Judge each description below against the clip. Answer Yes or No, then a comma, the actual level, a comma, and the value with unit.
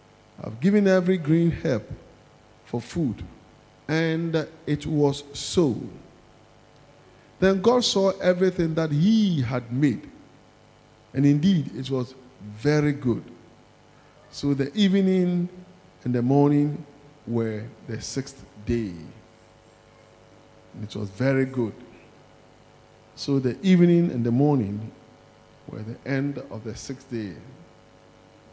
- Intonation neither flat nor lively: No, wide, 6.2 semitones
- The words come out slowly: Yes, slow, 110 wpm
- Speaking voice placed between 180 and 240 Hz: No, low, 135 Hz